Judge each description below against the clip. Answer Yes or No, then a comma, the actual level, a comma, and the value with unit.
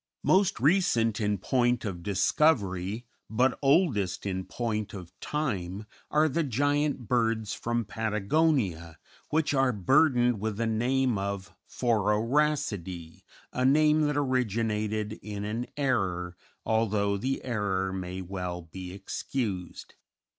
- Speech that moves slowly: Yes, slow, 120 wpm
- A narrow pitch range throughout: No, average, 5.3 semitones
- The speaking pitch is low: Yes, low, 110 Hz